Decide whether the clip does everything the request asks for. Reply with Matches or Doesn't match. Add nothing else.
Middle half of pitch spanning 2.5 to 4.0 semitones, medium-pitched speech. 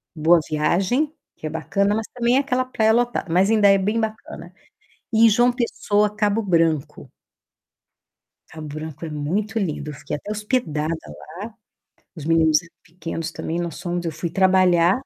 Doesn't match